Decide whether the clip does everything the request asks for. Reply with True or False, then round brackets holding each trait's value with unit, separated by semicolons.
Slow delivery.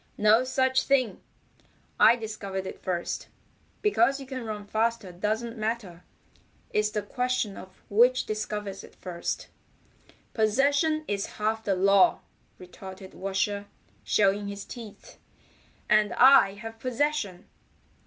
True (120 wpm)